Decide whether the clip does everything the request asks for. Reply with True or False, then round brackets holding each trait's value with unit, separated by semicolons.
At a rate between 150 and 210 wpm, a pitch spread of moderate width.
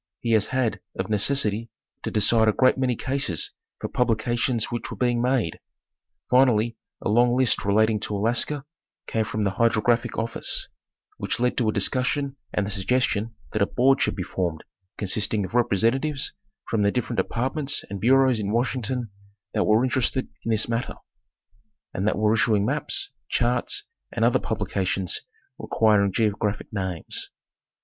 True (155 wpm; 3.1 semitones)